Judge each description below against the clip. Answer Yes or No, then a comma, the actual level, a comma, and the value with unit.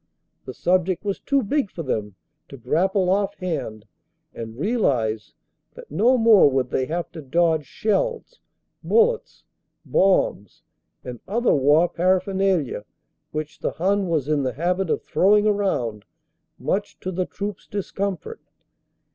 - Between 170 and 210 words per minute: No, slow, 135 wpm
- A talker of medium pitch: Yes, medium, 180 Hz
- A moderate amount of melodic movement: No, wide, 6.1 semitones